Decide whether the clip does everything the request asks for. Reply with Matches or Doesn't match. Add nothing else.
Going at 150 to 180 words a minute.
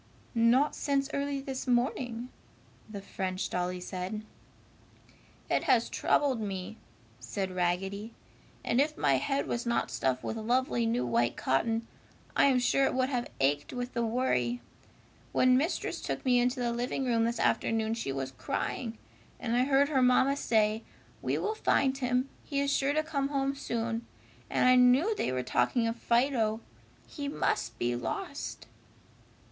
Matches